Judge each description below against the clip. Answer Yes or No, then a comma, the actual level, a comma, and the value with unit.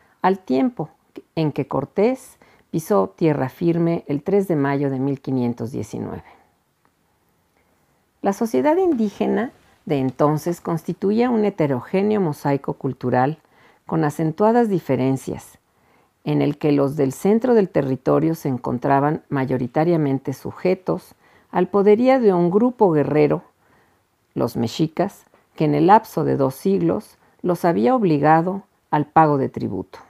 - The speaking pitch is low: No, medium, 160 Hz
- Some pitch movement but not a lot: No, wide, 5.7 semitones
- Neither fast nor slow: No, slow, 120 wpm